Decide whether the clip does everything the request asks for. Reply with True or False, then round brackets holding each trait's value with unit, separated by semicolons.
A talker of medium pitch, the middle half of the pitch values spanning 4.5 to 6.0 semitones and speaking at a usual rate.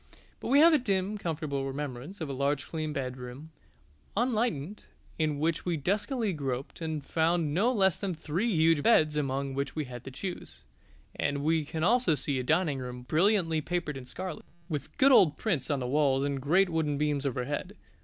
True (155 Hz; 4.8 semitones; 185 wpm)